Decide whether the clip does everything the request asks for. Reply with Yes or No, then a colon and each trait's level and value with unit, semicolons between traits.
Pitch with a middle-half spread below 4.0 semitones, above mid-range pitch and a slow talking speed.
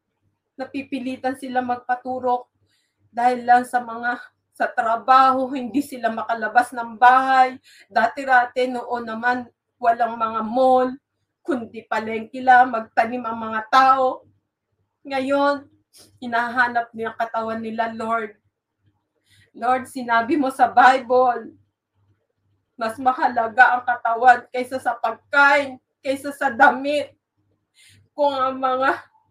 Yes: narrow, 2.5 semitones; high, 245 Hz; slow, 100 wpm